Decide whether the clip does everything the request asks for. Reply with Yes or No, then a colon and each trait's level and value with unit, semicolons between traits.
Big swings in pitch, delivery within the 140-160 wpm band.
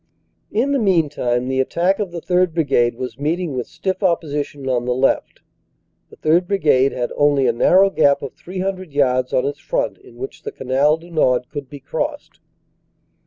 No: wide, 5.8 semitones; average, 185 wpm